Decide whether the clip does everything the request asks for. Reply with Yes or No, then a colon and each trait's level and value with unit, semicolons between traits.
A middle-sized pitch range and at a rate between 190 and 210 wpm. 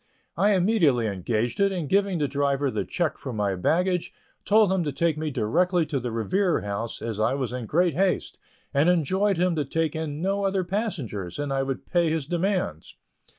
No: wide, 6.4 semitones; average, 195 wpm